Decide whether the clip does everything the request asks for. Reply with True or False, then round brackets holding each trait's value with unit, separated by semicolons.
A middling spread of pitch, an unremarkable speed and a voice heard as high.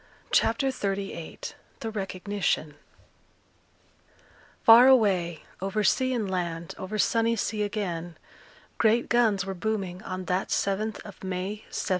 False (3.1 semitones; 120 wpm; 200 Hz)